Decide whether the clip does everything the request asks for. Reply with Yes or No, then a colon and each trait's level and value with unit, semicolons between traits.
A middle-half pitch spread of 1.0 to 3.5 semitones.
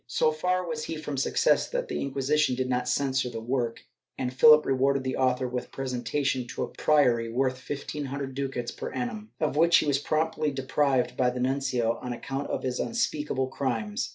Yes: average, 2.8 semitones